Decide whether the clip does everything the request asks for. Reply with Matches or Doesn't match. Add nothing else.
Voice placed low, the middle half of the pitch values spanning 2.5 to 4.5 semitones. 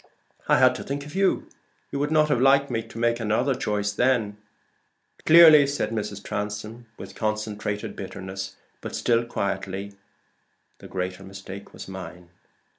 Doesn't match